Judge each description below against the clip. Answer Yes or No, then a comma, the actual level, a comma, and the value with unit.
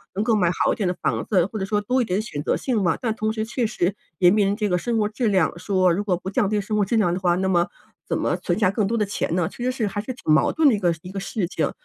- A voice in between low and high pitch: No, high, 205 Hz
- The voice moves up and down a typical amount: Yes, average, 3.1 semitones